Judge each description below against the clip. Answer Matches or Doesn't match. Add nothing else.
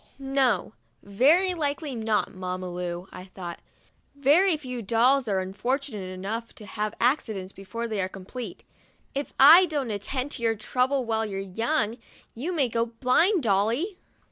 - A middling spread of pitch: Doesn't match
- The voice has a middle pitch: Doesn't match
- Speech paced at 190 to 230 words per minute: Doesn't match